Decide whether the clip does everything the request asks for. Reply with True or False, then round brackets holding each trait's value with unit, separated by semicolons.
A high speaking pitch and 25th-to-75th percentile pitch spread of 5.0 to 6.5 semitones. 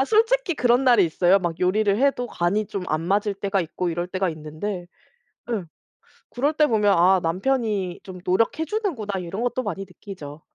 True (200 Hz; 5.3 semitones)